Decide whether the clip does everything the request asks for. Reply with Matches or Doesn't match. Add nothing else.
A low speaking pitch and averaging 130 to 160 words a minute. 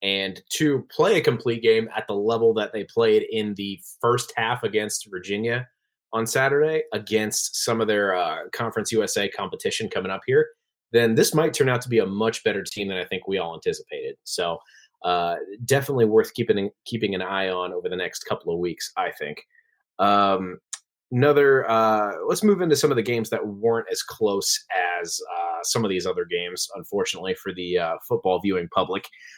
Doesn't match